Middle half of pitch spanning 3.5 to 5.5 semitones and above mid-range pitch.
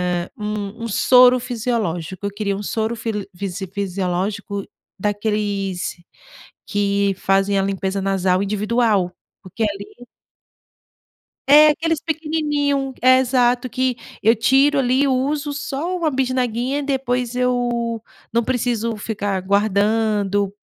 Yes: average, 4.2 semitones; high, 225 Hz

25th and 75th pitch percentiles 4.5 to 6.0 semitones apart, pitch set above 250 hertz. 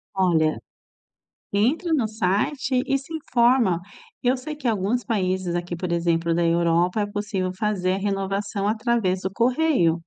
No: average, 5.0 semitones; high, 200 Hz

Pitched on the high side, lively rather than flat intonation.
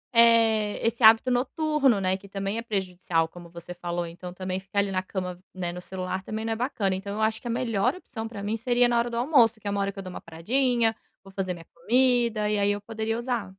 No: high, 210 Hz; average, 3.8 semitones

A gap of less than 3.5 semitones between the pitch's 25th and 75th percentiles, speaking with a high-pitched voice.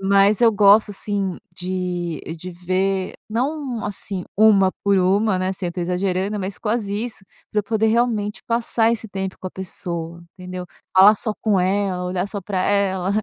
Yes: narrow, 2.4 semitones; high, 195 Hz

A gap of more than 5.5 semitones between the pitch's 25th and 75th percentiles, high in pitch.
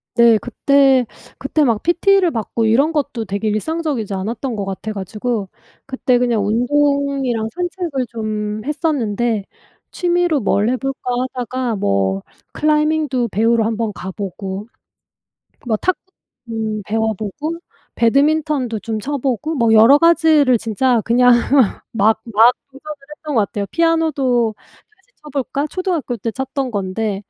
No: average, 5.1 semitones; high, 245 Hz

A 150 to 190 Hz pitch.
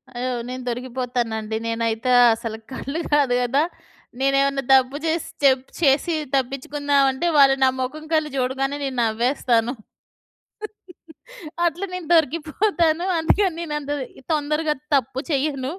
No: very high, 275 Hz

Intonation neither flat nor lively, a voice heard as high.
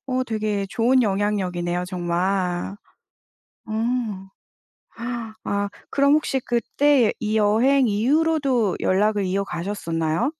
Yes: average, 4.8 semitones; high, 210 Hz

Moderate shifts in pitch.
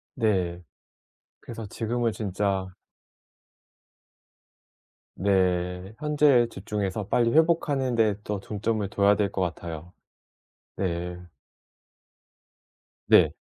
Yes: average, 4.0 semitones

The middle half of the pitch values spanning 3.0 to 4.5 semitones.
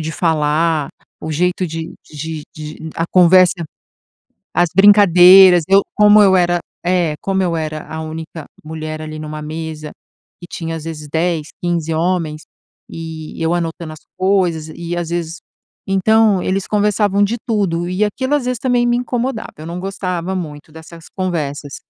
Yes: average, 3.3 semitones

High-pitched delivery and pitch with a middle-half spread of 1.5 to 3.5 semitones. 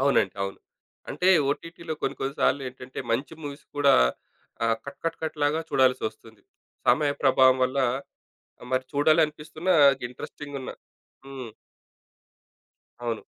No: medium, 140 Hz; average, 2.9 semitones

